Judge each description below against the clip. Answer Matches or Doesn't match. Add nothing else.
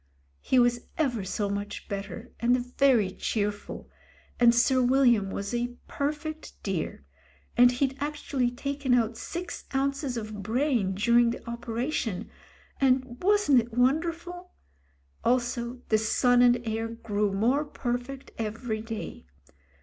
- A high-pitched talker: Matches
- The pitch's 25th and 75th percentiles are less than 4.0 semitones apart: Matches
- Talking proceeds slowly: Matches